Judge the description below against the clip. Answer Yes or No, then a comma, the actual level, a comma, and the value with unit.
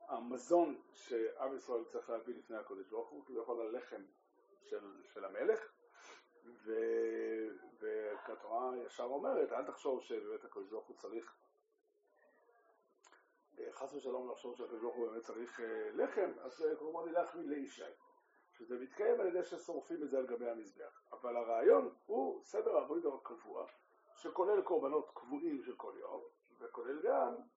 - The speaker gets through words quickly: No, average, 135 wpm